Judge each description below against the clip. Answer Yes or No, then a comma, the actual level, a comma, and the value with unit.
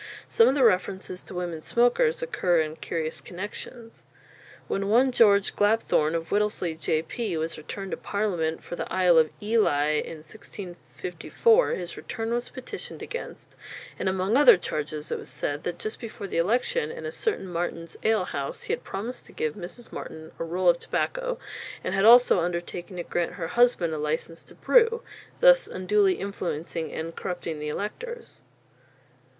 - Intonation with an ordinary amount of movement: No, wide, 5.9 semitones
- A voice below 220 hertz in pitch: Yes, medium, 185 Hz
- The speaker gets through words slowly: No, average, 165 wpm